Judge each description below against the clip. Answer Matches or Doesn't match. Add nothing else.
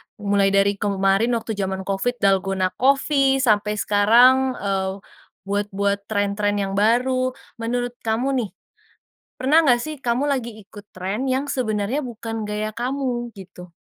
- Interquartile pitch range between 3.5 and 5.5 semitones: Matches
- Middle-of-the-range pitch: Doesn't match